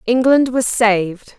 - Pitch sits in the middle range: No, high, 230 Hz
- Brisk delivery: No, slow, 130 wpm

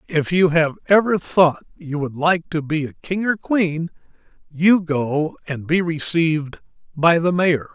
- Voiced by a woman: No, male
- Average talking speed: Yes, average, 170 wpm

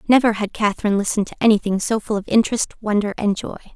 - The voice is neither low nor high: No, high, 210 Hz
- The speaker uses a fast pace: Yes, fast, 210 wpm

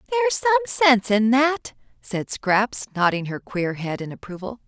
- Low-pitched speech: No, high, 240 Hz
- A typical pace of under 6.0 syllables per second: No, 6.1 syllables/s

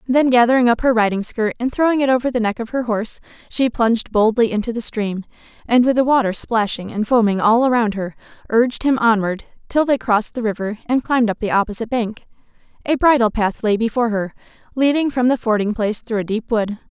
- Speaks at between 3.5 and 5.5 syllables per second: No, 6.1 syllables/s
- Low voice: No, high, 230 Hz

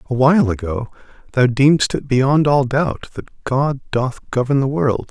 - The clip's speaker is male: Yes, male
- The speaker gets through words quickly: No, average, 165 wpm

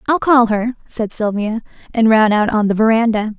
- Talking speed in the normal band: Yes, average, 195 wpm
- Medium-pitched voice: No, high, 225 Hz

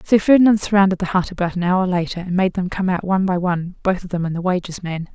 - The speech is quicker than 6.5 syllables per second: Yes, 6.7 syllables/s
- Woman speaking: Yes, female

